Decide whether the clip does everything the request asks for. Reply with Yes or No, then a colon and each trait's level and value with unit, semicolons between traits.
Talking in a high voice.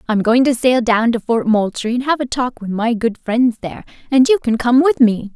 Yes: high, 245 Hz